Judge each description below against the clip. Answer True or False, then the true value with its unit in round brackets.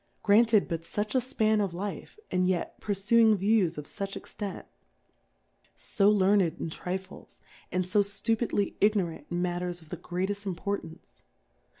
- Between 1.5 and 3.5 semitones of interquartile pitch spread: True (2.9 semitones)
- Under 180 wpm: True (140 wpm)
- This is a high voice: True (195 Hz)